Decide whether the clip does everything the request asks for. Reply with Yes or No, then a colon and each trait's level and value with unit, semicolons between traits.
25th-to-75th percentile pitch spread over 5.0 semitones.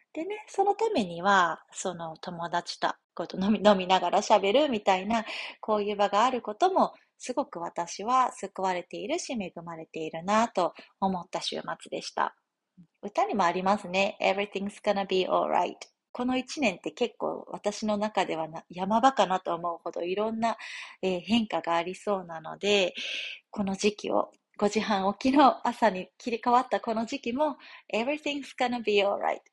No: average, 4.7 semitones